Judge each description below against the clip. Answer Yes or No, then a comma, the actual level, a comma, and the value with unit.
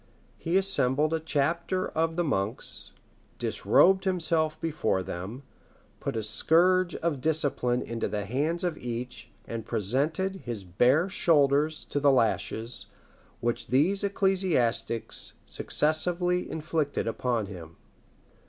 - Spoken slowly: Yes, slow, 115 wpm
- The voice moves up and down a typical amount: No, wide, 6.2 semitones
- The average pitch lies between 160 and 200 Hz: No, medium, 150 Hz